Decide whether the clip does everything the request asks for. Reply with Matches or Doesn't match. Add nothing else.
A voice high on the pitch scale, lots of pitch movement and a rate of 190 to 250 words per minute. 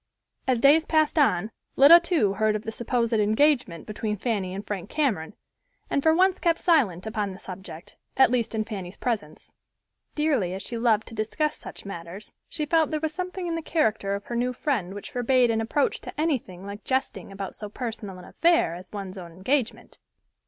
Matches